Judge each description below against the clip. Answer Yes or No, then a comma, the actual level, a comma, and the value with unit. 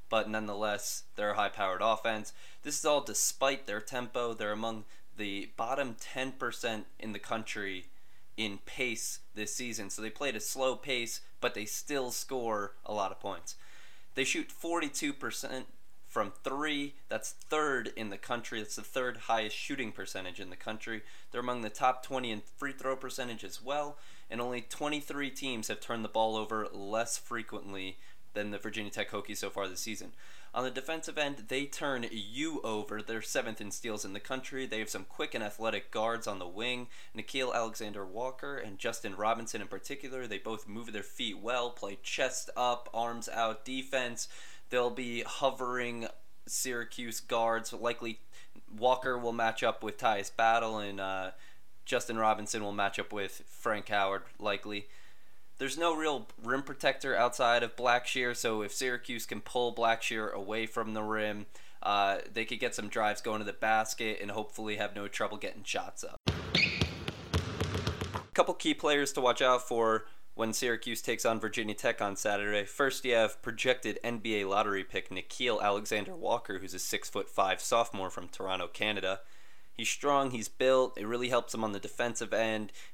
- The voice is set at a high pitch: No, low, 115 Hz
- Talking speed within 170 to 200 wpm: Yes, average, 175 wpm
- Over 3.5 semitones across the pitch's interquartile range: No, average, 3.2 semitones